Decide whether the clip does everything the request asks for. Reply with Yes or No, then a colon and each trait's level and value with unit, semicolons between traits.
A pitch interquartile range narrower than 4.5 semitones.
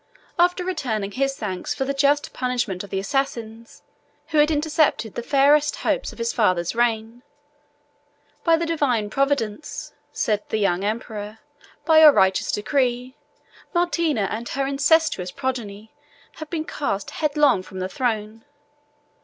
No: wide, 5.5 semitones